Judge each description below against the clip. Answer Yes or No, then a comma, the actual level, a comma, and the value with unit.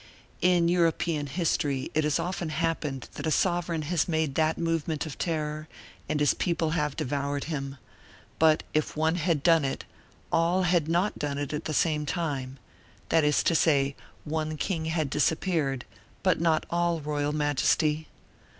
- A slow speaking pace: No, average, 160 wpm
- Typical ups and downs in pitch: No, narrow, 2.3 semitones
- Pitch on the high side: No, medium, 155 Hz